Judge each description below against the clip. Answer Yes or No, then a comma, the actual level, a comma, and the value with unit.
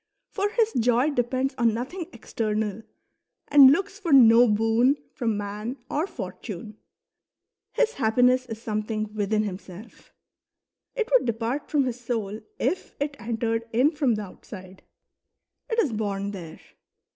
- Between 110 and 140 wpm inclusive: Yes, slow, 135 wpm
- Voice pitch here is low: No, high, 230 Hz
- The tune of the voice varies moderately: Yes, average, 4.4 semitones